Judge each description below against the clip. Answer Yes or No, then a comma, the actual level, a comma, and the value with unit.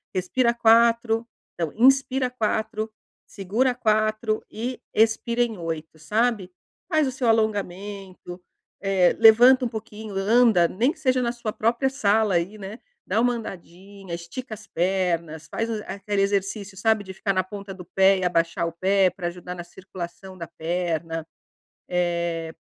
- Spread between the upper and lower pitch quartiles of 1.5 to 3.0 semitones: No, average, 4.1 semitones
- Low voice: No, high, 205 Hz